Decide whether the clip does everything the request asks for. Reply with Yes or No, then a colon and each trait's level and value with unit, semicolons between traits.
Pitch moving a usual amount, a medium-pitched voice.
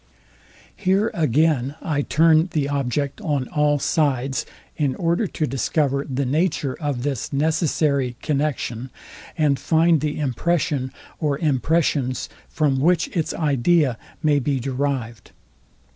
Yes: average, 3.0 semitones; medium, 145 Hz